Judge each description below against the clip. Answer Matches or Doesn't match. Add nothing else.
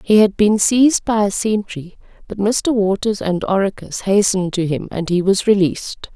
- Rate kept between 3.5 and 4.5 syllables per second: Doesn't match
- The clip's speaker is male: Doesn't match